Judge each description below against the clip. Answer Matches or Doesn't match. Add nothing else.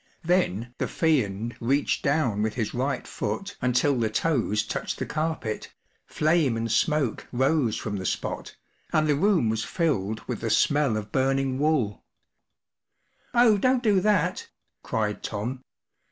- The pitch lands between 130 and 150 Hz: Matches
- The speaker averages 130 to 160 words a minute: Matches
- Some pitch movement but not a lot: Doesn't match